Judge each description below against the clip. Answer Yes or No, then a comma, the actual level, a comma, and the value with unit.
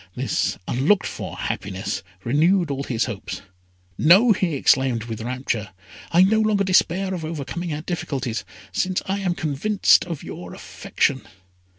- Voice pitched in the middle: Yes, medium, 160 Hz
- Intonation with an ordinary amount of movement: No, wide, 6.7 semitones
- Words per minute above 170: No, average, 145 wpm